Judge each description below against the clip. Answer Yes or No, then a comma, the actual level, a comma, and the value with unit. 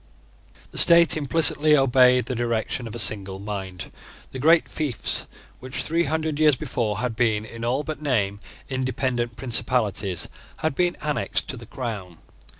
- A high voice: No, low, 125 Hz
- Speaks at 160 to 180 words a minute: No, average, 150 wpm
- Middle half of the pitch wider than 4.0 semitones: Yes, average, 5.1 semitones